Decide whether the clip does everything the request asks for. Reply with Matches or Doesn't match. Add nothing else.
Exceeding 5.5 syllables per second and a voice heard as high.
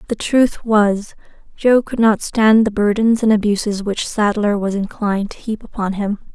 Doesn't match